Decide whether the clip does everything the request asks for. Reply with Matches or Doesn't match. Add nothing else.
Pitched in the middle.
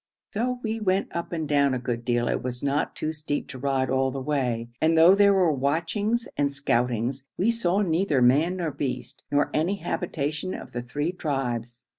Matches